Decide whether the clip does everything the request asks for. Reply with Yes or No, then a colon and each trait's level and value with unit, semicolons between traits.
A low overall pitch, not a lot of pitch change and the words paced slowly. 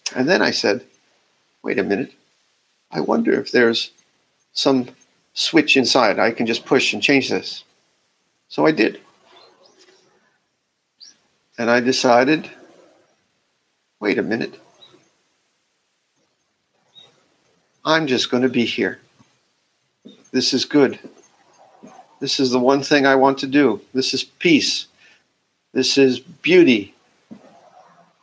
Yes: low, 130 Hz; narrow, 1.9 semitones; slow, 115 wpm